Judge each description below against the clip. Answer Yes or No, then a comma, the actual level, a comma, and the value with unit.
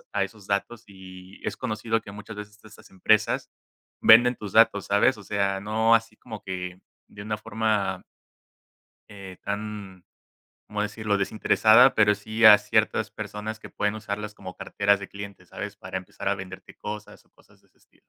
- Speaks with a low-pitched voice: Yes, low, 105 Hz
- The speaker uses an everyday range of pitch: No, narrow, 1.5 semitones